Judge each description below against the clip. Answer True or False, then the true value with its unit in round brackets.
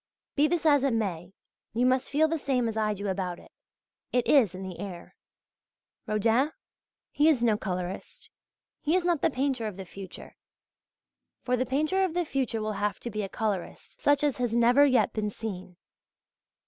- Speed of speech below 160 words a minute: False (185 wpm)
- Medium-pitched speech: False (235 Hz)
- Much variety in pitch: True (5.8 semitones)